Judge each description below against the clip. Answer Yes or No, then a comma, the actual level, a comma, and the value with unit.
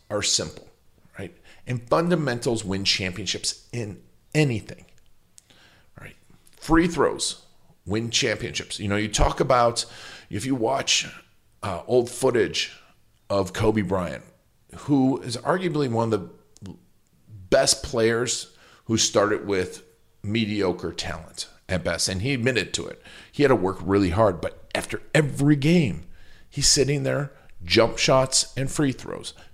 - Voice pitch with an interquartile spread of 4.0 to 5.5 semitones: Yes, average, 4.8 semitones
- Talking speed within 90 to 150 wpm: Yes, slow, 135 wpm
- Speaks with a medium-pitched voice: No, low, 115 Hz